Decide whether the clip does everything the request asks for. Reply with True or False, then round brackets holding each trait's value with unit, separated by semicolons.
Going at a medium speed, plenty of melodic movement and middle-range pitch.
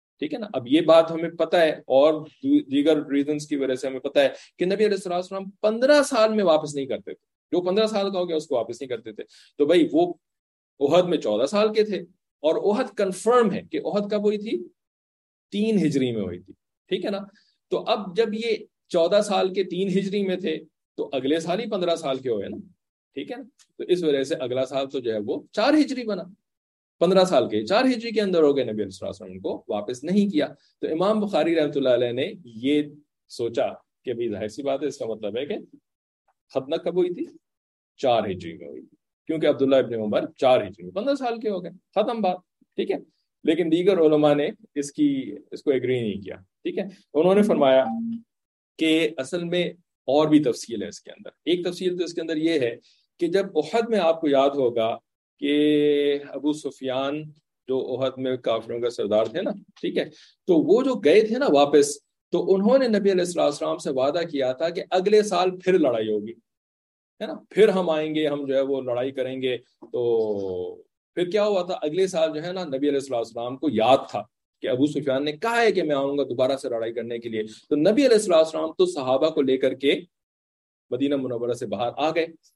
False (220 wpm; 7.2 semitones; 165 Hz)